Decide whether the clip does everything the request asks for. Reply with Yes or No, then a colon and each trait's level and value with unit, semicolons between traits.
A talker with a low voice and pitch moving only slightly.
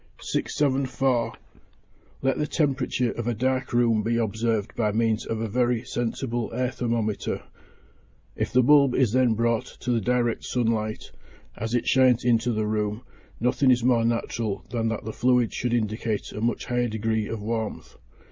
Yes: low, 115 Hz; narrow, 2.0 semitones